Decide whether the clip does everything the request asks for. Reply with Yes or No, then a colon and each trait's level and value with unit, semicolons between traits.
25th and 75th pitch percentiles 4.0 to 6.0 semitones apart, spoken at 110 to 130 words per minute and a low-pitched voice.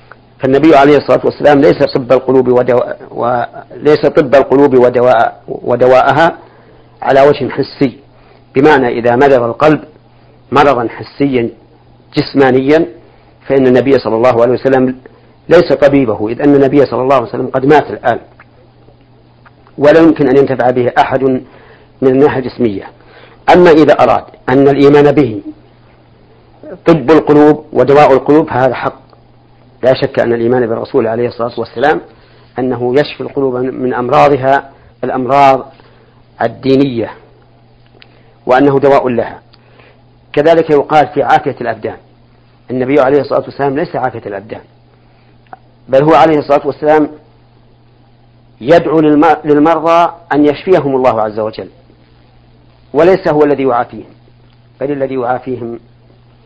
No: average, 3.1 semitones; average, 120 wpm; low, 130 Hz